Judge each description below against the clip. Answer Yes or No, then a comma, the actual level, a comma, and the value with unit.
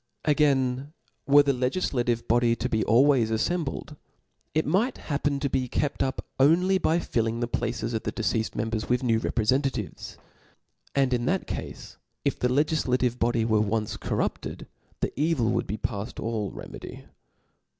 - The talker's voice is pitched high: No, low, 125 Hz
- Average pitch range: Yes, average, 3.9 semitones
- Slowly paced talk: No, average, 155 wpm